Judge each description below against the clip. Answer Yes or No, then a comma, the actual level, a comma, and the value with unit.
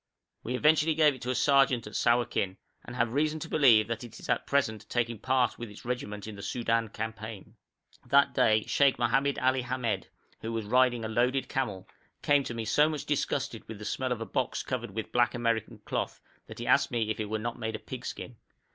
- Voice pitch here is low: Yes, low, 120 Hz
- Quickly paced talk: Yes, fast, 220 wpm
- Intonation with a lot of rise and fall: No, average, 3.0 semitones